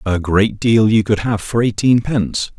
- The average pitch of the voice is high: No, low, 105 Hz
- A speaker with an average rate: Yes, average, 185 wpm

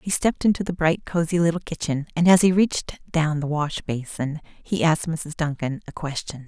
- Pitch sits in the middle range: Yes, medium, 160 Hz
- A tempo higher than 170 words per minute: Yes, fast, 205 wpm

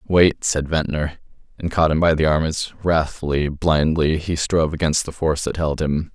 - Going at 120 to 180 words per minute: No, average, 195 wpm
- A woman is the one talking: No, male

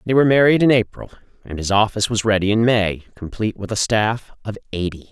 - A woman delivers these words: No, male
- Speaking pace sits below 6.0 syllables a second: No, 6.4 syllables/s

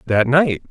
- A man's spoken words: Yes, male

